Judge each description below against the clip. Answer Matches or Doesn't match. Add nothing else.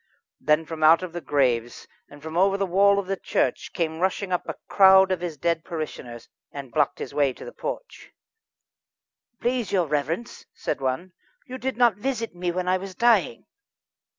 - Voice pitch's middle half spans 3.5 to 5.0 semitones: Matches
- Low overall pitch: Doesn't match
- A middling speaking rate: Matches